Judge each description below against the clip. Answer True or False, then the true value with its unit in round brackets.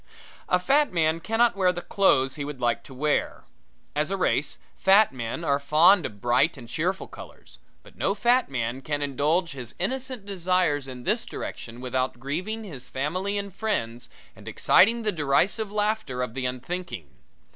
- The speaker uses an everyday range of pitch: False (7.1 semitones)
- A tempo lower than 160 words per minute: False (170 wpm)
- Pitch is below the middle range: False (160 Hz)